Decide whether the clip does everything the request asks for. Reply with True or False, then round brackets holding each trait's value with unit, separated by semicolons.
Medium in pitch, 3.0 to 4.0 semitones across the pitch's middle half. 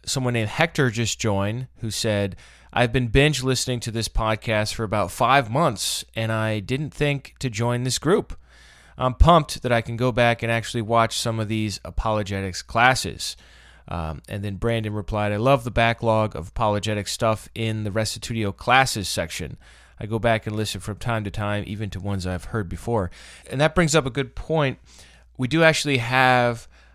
False (110 Hz; 3.4 semitones)